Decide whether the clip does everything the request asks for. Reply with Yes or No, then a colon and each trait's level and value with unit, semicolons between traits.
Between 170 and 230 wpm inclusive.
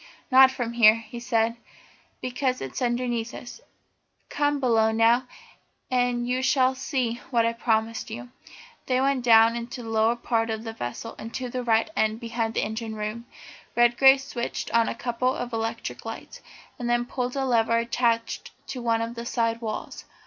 Yes: average, 175 wpm